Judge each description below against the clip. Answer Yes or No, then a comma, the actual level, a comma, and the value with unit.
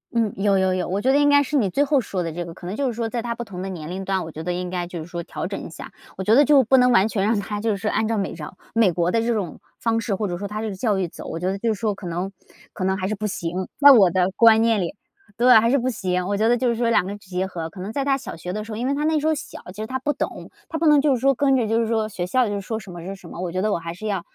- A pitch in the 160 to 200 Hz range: No, high, 210 Hz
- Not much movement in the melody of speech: No, average, 4.3 semitones